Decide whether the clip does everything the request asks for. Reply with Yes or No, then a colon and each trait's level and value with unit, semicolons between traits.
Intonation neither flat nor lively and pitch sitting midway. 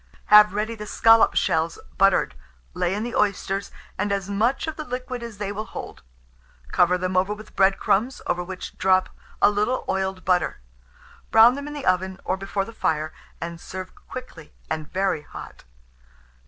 No: average, 3.1 semitones; high, 195 Hz